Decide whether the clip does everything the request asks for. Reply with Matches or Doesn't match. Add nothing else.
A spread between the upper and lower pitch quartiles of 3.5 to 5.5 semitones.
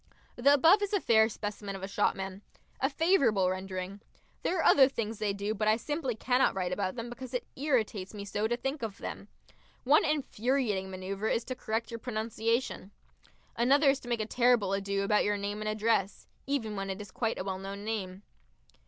Matches